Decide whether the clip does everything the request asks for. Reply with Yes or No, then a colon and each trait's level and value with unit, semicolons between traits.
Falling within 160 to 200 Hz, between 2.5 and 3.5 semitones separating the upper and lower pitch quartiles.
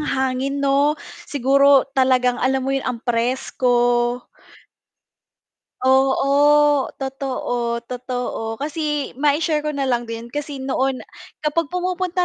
No: very high, 270 Hz; average, 2.8 semitones